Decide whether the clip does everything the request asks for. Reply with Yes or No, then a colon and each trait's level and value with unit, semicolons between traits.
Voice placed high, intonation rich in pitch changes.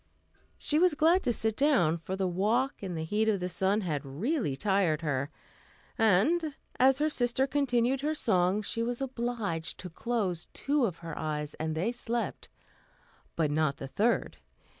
Yes: high, 210 Hz; wide, 7.3 semitones